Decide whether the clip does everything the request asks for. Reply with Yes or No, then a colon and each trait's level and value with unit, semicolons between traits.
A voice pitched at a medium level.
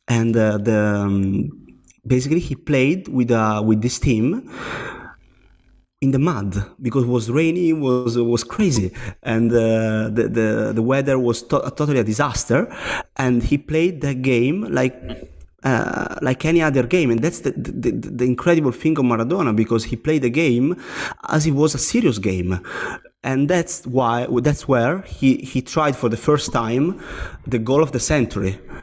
No: low, 125 Hz